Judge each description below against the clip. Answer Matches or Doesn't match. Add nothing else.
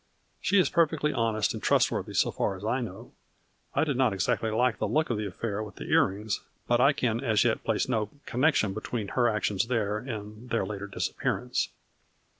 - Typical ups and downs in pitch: Matches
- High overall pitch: Doesn't match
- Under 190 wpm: Doesn't match